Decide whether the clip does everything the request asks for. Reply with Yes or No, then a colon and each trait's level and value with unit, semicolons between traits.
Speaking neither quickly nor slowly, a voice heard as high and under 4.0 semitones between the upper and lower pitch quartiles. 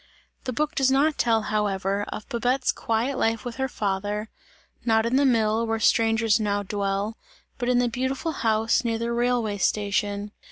Yes: average, 170 wpm; high, 225 Hz; average, 2.9 semitones